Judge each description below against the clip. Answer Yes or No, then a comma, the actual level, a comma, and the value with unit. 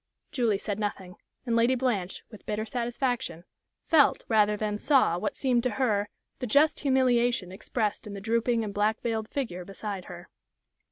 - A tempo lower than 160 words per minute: No, average, 165 wpm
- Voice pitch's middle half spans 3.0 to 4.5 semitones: Yes, average, 3.4 semitones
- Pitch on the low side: No, high, 220 Hz